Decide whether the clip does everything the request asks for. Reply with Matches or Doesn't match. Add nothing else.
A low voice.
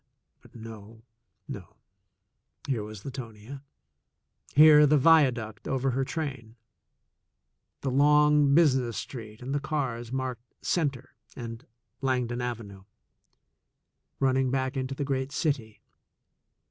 Matches